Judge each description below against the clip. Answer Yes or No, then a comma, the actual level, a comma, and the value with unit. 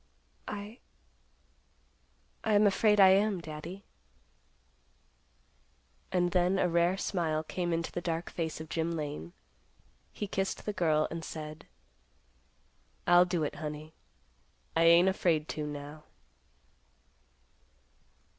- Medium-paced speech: No, slow, 110 wpm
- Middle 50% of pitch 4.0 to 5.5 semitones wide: No, average, 3.4 semitones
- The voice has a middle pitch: Yes, medium, 170 Hz